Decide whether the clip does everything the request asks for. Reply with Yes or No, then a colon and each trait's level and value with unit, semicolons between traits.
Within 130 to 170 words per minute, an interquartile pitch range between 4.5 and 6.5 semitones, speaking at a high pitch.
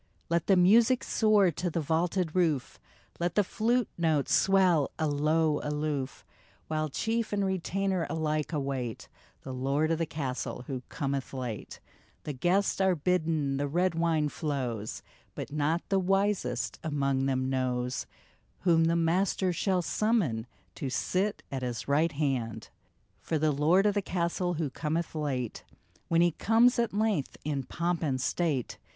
No: average, 150 wpm; average, 4.8 semitones; medium, 160 Hz